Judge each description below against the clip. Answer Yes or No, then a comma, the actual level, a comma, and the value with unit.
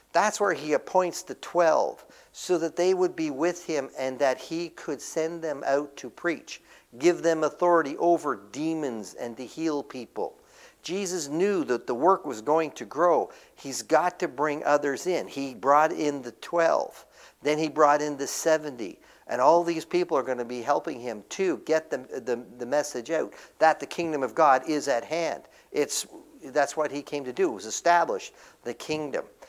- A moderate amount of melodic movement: Yes, average, 3.6 semitones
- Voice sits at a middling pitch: Yes, medium, 155 Hz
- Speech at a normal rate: Yes, average, 190 wpm